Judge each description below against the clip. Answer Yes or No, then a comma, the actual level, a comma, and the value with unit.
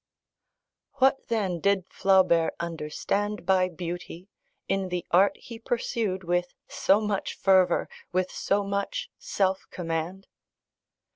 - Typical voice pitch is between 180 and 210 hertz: Yes, high, 190 Hz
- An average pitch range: No, narrow, 2.2 semitones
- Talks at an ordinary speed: No, slow, 115 wpm